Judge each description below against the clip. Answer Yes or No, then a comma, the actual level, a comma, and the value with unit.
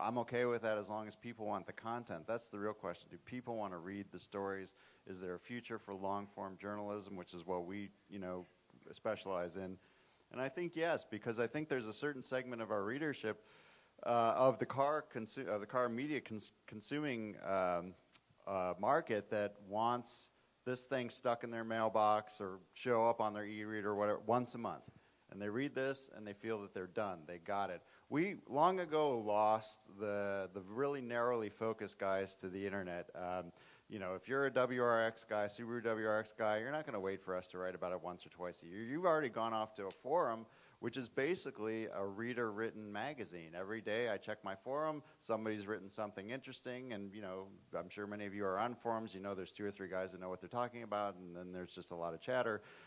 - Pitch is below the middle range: Yes, low, 105 Hz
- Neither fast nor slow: No, fast, 220 wpm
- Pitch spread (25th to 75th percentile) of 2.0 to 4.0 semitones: Yes, average, 3.6 semitones